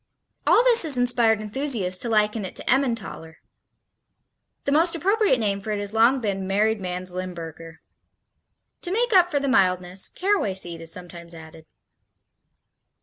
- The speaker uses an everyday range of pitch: No, wide, 7.1 semitones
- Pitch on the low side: No, high, 210 Hz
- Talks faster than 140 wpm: Yes, average, 150 wpm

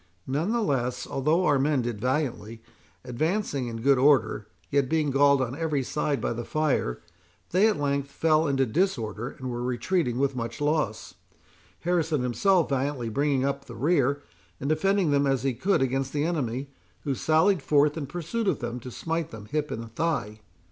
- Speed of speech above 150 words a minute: Yes, average, 175 wpm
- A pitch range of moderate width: Yes, average, 3.9 semitones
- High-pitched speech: No, medium, 140 Hz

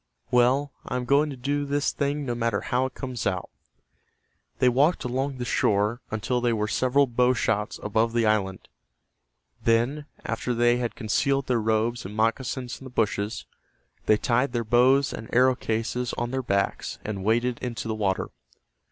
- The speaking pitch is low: Yes, low, 120 Hz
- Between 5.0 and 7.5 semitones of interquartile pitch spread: No, average, 2.9 semitones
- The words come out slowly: No, average, 175 wpm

